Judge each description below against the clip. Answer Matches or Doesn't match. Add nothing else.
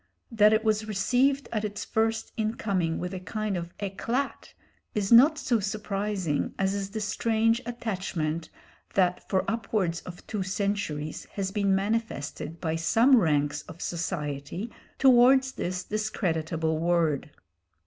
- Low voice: Doesn't match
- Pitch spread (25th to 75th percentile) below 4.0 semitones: Doesn't match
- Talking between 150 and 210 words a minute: Doesn't match